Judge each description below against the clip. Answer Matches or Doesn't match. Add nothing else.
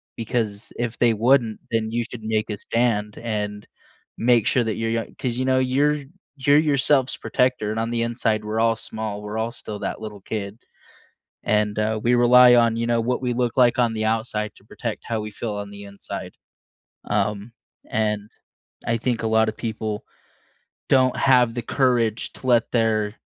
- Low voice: Matches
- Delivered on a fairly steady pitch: Matches